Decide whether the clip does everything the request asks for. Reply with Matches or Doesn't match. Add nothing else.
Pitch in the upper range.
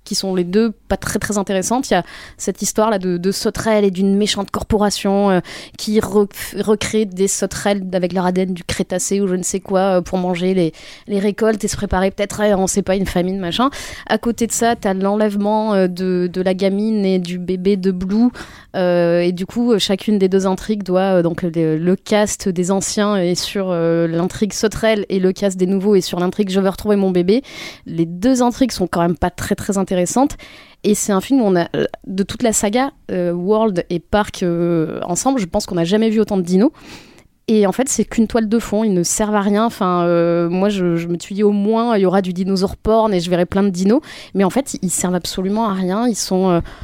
Matches